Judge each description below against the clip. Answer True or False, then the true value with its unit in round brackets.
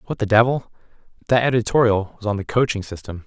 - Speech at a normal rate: True (165 wpm)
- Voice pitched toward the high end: False (110 Hz)